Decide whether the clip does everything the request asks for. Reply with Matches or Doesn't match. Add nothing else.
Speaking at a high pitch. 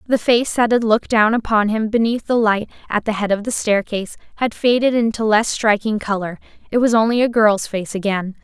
Matches